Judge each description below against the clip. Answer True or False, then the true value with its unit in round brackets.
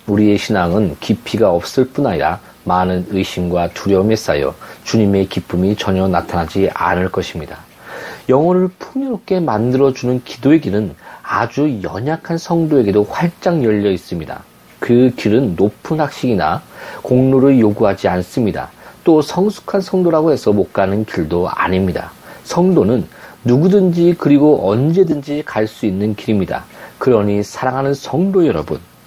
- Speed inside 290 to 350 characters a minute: True (315 characters per minute)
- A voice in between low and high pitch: False (110 Hz)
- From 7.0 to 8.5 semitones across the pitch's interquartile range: True (8.0 semitones)